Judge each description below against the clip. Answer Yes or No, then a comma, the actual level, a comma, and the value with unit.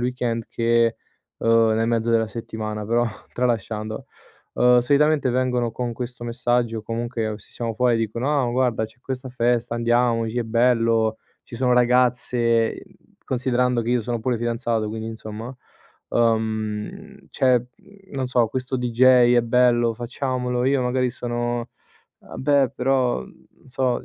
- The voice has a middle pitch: No, low, 120 Hz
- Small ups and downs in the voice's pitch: Yes, narrow, 1.6 semitones